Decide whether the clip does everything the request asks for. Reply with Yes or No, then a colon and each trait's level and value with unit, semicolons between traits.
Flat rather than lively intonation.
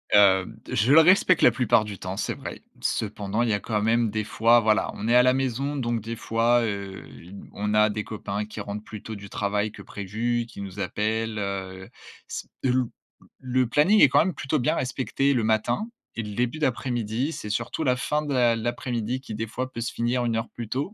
No: average, 3.3 semitones